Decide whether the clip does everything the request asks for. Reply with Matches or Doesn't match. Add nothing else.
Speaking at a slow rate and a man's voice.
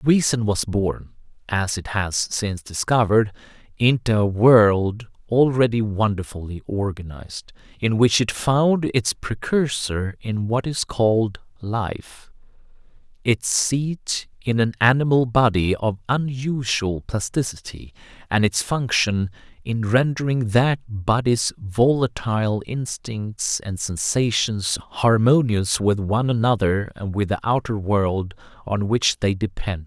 Matches